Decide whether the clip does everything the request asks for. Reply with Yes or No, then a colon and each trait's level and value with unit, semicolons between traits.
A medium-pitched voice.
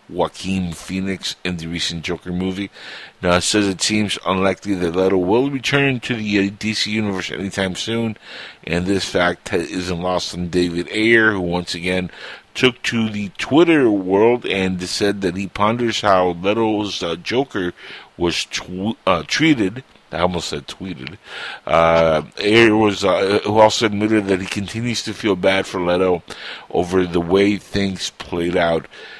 No: very low, 95 Hz